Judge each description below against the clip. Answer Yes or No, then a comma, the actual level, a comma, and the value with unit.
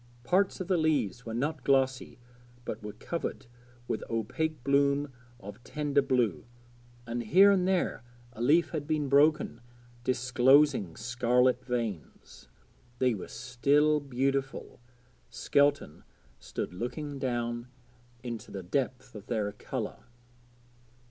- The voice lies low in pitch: Yes, low, 130 Hz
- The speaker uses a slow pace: Yes, slow, 115 wpm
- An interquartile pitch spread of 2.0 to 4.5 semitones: Yes, average, 3.6 semitones